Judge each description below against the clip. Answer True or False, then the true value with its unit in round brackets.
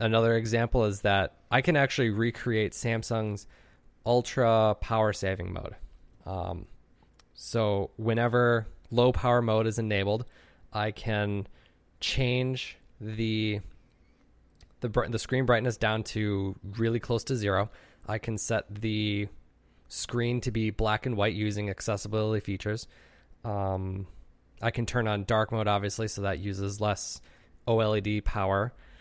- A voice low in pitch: True (105 Hz)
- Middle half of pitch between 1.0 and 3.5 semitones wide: True (2.8 semitones)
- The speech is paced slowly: True (130 wpm)